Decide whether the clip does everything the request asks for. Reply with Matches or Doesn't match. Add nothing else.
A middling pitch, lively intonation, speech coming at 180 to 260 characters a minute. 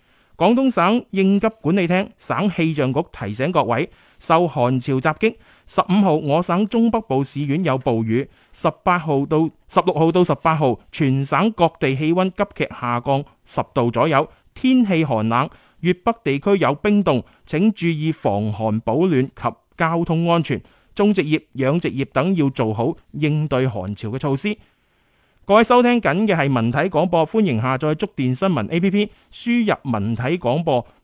Matches